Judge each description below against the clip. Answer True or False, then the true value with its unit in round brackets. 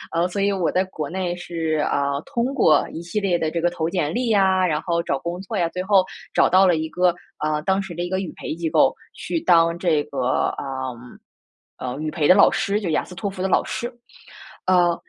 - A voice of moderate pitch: True (175 Hz)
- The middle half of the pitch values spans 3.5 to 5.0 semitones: False (3.1 semitones)